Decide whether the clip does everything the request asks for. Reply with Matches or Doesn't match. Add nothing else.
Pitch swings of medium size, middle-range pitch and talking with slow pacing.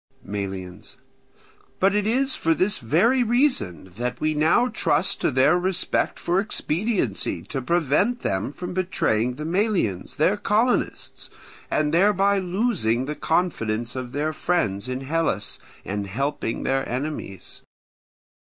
Doesn't match